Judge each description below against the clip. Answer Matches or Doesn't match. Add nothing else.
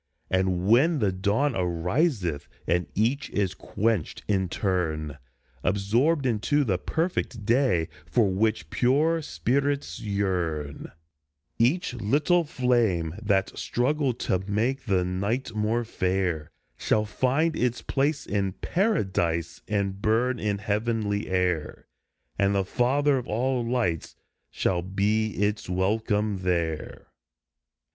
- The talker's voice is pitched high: Doesn't match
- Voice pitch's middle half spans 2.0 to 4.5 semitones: Doesn't match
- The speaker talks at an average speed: Doesn't match